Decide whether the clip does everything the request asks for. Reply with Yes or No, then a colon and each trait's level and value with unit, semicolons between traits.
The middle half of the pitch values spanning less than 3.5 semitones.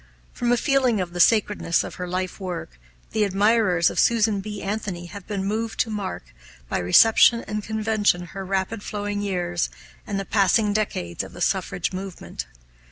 Yes: average, 2.9 semitones